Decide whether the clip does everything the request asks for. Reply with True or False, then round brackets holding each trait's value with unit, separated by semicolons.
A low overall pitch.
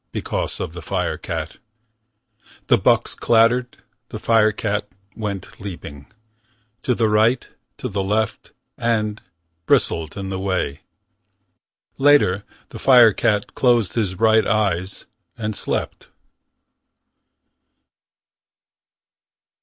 True (105 Hz)